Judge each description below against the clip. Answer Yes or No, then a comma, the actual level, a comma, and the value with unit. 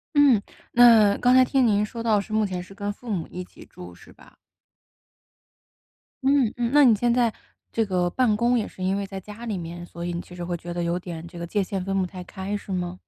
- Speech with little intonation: No, average, 4.5 semitones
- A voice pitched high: Yes, high, 200 Hz